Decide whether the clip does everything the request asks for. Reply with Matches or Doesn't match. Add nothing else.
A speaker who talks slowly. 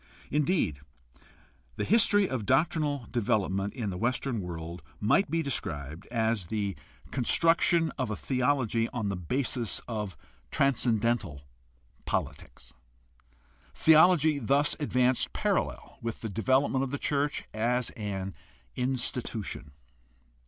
Matches